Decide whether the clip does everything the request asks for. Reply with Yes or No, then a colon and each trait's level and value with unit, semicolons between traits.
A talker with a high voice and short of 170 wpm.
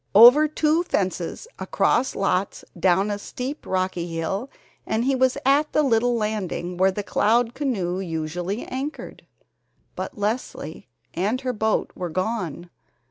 Yes: high, 210 Hz; slow, 135 wpm